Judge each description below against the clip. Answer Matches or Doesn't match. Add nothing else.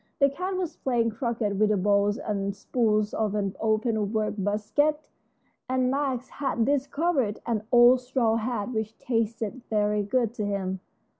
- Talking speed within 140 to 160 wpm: Matches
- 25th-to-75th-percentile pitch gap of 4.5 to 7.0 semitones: Doesn't match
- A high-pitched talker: Matches